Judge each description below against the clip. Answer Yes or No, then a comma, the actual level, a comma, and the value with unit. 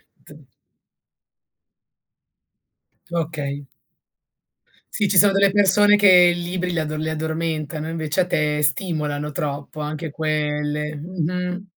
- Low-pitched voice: No, medium, 160 Hz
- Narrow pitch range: No, average, 3.2 semitones